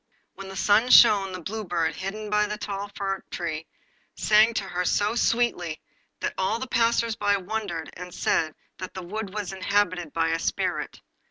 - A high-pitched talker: Yes, high, 195 Hz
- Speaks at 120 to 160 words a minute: No, average, 175 wpm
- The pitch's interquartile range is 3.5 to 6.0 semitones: No, average, 3.1 semitones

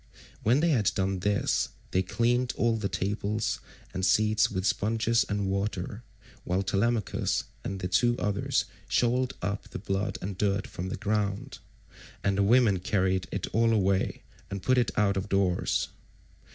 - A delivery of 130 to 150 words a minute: No, average, 160 wpm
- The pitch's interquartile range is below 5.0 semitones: Yes, average, 2.8 semitones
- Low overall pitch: Yes, low, 100 Hz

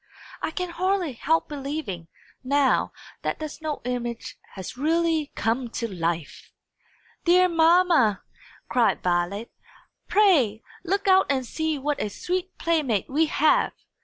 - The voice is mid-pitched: No, very high, 295 Hz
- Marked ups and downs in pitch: Yes, wide, 6.4 semitones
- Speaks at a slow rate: Yes, slow, 130 wpm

